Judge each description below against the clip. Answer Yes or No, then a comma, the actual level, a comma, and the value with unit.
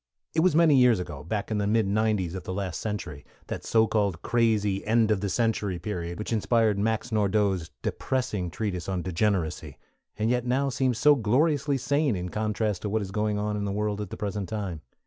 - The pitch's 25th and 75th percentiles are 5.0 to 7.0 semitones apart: No, average, 2.8 semitones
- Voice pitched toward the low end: Yes, low, 105 Hz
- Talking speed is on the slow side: No, fast, 205 wpm